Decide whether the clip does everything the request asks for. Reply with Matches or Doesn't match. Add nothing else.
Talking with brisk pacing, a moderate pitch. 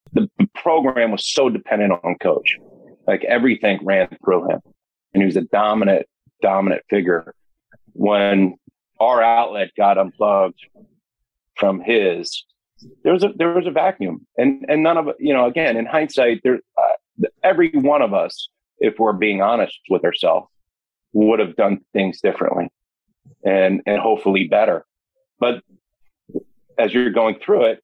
Doesn't match